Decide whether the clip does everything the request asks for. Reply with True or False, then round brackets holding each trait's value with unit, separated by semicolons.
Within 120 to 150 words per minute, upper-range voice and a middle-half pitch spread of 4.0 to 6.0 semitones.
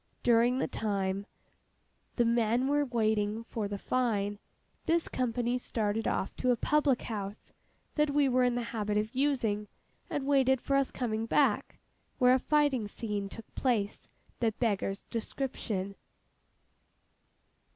False (140 wpm; 235 Hz; 3.5 semitones)